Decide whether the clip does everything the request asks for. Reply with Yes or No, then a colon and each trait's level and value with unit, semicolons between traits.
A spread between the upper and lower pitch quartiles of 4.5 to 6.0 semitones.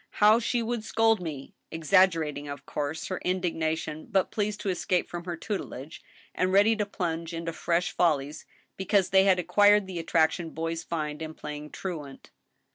No: average, 3.6 semitones